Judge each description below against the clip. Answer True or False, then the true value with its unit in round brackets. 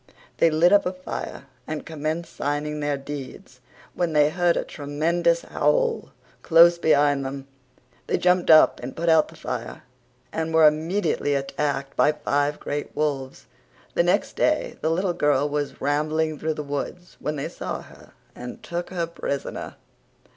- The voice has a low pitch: False (155 Hz)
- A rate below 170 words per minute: True (160 wpm)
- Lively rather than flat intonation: False (2.7 semitones)